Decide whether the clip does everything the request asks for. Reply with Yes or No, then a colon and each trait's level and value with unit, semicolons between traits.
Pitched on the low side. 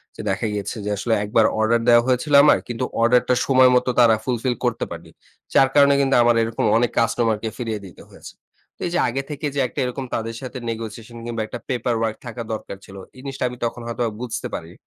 Yes: low, 120 Hz